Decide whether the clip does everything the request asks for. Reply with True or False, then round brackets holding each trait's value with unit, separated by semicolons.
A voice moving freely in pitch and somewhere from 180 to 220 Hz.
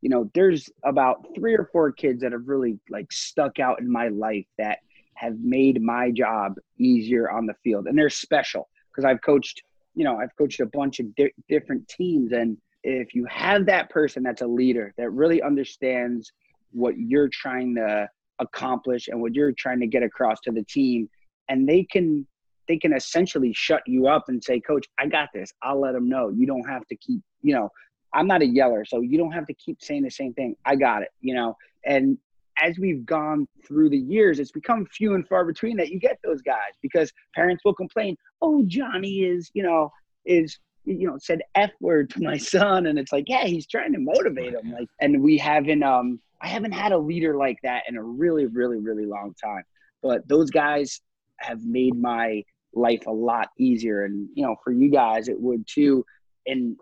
False (7.3 semitones; 140 Hz)